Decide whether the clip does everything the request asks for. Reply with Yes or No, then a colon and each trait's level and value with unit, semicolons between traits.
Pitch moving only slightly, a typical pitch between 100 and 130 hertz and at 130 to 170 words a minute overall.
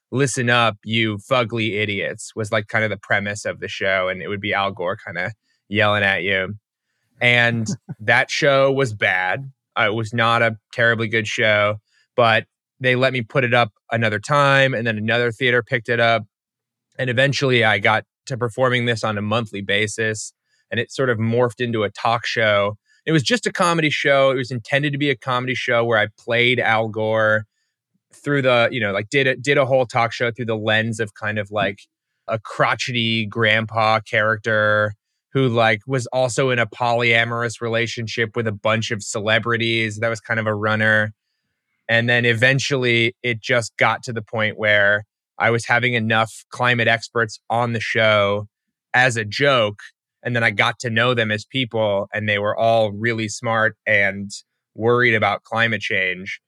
No: narrow, 2.3 semitones; low, 115 Hz; average, 185 wpm